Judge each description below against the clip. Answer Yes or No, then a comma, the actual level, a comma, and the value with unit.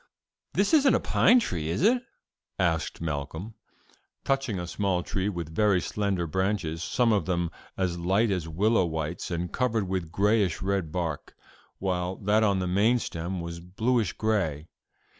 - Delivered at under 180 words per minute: Yes, average, 160 wpm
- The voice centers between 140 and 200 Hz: No, very low, 95 Hz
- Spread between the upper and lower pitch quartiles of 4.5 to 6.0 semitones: No, average, 3.9 semitones